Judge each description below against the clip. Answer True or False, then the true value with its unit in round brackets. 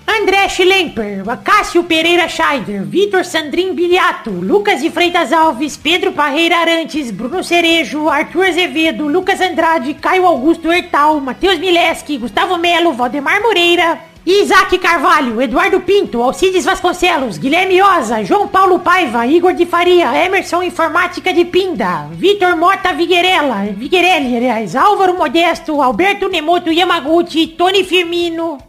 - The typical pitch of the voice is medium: False (345 Hz)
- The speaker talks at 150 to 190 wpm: False (120 wpm)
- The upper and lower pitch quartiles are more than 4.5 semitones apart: False (2.6 semitones)